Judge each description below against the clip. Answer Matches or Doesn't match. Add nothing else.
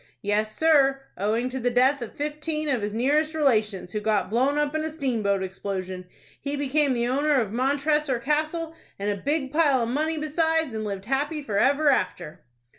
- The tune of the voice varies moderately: Doesn't match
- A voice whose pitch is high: Matches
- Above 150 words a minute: Matches